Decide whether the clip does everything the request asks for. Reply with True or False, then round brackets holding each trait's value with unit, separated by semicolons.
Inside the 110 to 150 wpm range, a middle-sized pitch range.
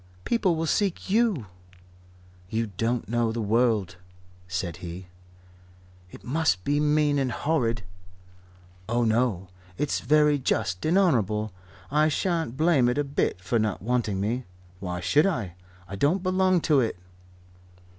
False (140 wpm; 6.4 semitones)